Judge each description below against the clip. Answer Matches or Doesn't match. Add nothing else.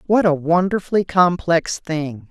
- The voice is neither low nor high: Matches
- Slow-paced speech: Matches